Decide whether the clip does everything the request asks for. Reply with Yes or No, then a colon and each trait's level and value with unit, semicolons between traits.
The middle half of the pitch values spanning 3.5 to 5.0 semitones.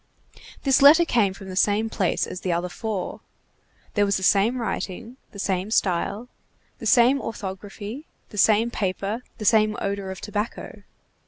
No: average, 3.0 semitones